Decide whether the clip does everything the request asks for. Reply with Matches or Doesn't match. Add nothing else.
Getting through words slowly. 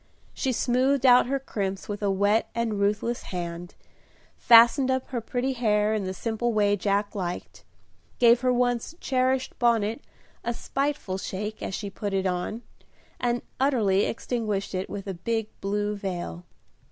Doesn't match